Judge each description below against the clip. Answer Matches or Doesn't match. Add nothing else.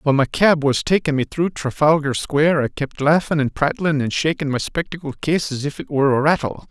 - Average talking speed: Doesn't match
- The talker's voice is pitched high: Doesn't match